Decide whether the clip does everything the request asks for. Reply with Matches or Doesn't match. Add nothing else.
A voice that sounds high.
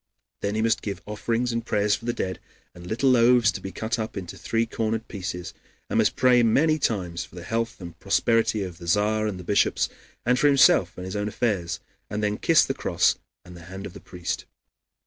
Doesn't match